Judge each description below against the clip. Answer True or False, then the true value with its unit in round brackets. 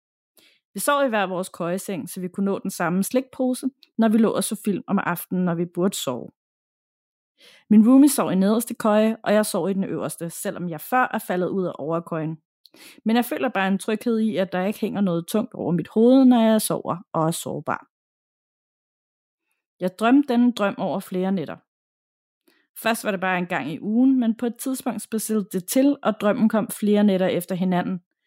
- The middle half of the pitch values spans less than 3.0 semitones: False (3.9 semitones)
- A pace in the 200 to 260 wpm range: True (205 wpm)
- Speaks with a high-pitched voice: True (205 Hz)